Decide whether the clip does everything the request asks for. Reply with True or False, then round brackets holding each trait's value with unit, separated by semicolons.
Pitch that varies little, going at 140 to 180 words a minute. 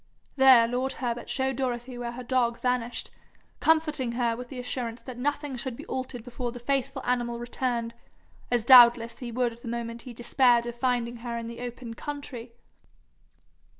True (1.5 semitones; 170 wpm)